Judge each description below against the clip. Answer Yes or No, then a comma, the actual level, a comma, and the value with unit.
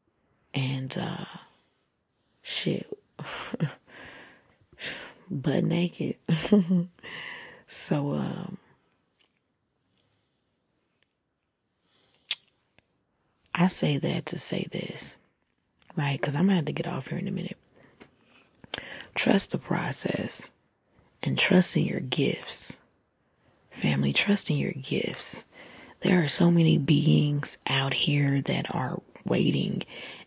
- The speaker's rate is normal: No, slow, 95 wpm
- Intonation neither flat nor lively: Yes, average, 4.2 semitones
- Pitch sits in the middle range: Yes, medium, 170 Hz